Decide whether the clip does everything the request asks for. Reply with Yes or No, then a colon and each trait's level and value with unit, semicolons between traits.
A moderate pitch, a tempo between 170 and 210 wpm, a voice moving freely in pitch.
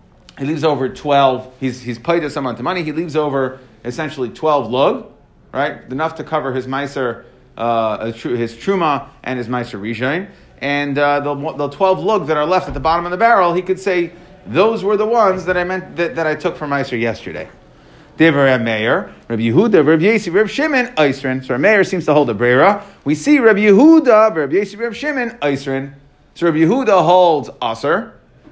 Yes: medium, 155 Hz; average, 190 wpm; wide, 6.1 semitones